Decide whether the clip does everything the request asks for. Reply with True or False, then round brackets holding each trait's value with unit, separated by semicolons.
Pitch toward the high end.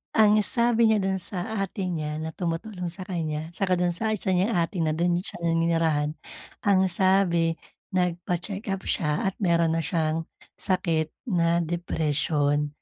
False (175 Hz)